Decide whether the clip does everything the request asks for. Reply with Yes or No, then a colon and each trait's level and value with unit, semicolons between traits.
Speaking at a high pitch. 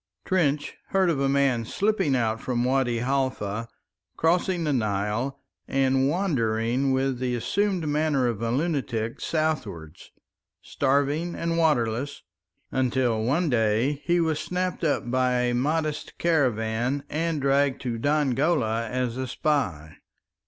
No: low, 135 Hz